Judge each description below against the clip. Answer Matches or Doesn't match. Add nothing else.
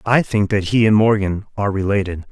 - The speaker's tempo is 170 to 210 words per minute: Matches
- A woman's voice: Doesn't match